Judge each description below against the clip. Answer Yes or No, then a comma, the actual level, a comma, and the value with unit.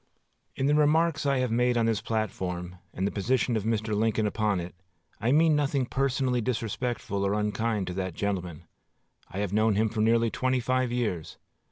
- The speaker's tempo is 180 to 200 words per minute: Yes, average, 185 wpm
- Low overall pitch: Yes, low, 110 Hz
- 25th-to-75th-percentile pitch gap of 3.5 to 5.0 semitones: Yes, average, 4.0 semitones